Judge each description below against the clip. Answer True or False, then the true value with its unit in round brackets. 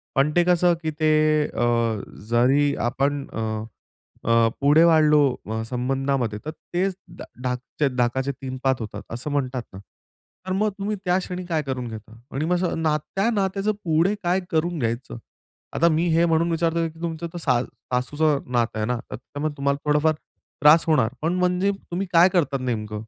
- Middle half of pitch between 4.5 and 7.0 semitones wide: True (5.2 semitones)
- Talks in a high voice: False (150 Hz)